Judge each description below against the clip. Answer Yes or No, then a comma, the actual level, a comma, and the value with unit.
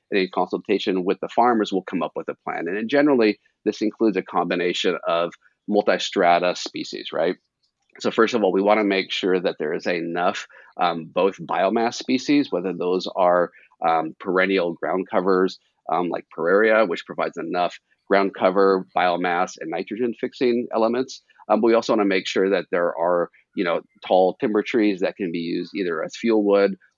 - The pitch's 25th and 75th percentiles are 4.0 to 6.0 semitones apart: No, average, 3.4 semitones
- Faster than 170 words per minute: Yes, average, 180 wpm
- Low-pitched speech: Yes, low, 100 Hz